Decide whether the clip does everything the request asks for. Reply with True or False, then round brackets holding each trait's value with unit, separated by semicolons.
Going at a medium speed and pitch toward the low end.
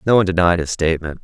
False (245 wpm; 85 Hz)